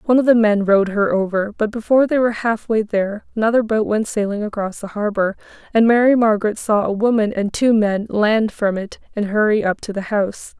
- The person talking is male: No, female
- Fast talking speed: Yes, fast, 215 wpm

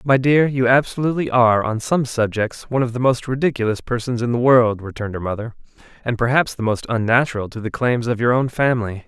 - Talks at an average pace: No, fast, 210 wpm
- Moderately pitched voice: No, low, 120 Hz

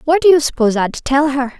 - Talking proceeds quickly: Yes, fast, 265 wpm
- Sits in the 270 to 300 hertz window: Yes, very high, 280 Hz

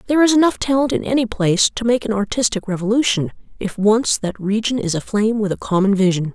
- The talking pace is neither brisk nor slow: No, fast, 210 wpm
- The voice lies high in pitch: Yes, high, 215 Hz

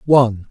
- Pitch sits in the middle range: No, low, 120 Hz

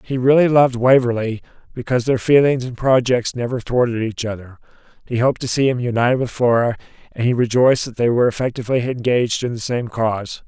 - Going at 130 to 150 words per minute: No, average, 190 wpm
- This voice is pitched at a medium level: No, low, 120 Hz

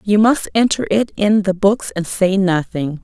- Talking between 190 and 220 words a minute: Yes, average, 200 wpm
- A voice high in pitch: Yes, high, 200 Hz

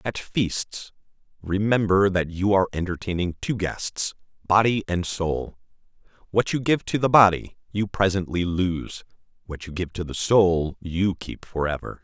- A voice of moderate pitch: No, very low, 95 Hz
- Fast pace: No, average, 155 wpm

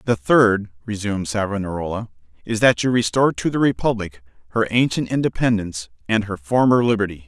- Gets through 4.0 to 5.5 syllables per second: No, 5.9 syllables/s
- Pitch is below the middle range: Yes, low, 105 Hz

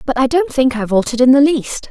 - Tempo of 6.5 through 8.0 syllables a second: Yes, 6.6 syllables/s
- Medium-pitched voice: No, very high, 260 Hz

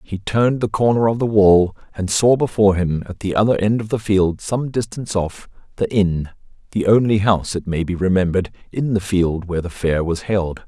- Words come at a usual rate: No, fast, 210 wpm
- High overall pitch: No, low, 100 Hz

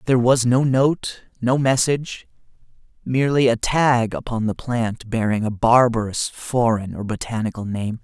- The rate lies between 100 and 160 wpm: Yes, average, 140 wpm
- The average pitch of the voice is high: No, low, 120 Hz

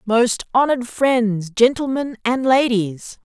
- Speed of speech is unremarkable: No, slow, 110 wpm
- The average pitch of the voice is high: Yes, high, 240 Hz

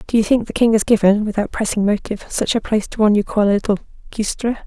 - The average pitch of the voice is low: No, high, 215 Hz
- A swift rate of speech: Yes, fast, 255 wpm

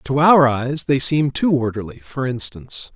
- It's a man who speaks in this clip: Yes, male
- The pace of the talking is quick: No, average, 185 wpm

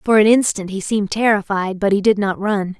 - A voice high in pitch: Yes, high, 200 Hz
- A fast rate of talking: Yes, fast, 235 wpm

